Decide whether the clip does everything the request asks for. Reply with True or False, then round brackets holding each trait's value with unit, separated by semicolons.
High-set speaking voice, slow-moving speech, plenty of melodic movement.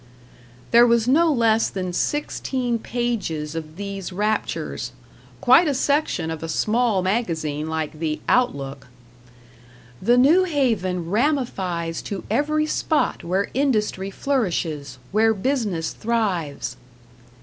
True (210 Hz; 115 wpm; 7.1 semitones)